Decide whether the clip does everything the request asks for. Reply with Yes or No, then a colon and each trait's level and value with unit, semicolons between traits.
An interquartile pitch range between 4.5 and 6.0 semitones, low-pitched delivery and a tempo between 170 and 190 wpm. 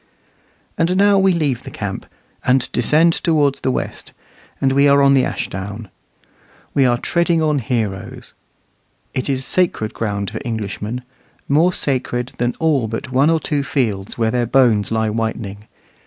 No: average, 4.8 semitones; low, 130 Hz; average, 155 wpm